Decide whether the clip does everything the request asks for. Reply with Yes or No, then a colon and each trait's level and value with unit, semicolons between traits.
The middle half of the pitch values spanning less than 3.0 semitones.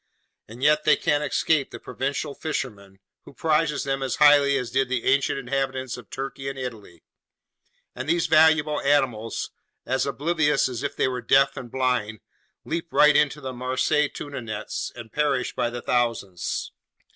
No: average, 3.3 semitones